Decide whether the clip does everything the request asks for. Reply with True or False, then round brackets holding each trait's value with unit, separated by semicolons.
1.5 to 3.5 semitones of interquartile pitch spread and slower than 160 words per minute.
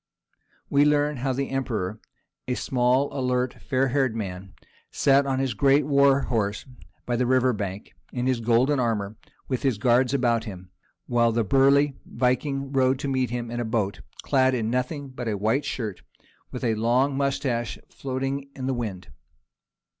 False (2.8 semitones; 170 wpm)